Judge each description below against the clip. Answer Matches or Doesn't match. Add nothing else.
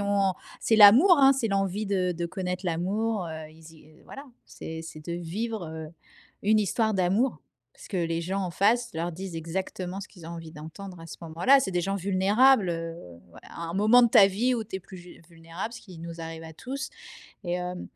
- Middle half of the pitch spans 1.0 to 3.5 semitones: Doesn't match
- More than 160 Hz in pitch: Matches